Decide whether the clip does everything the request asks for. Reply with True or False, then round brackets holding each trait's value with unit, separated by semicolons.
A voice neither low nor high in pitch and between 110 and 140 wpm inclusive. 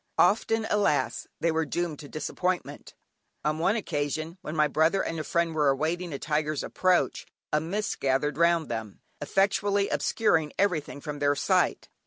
False (160 Hz; 160 wpm)